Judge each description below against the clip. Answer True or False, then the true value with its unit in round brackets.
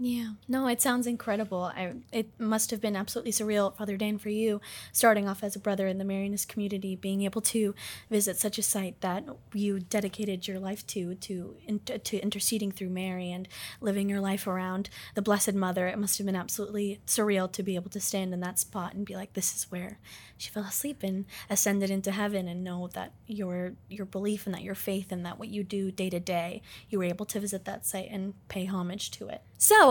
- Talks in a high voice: True (200 Hz)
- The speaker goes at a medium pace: False (220 wpm)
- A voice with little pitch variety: True (1.9 semitones)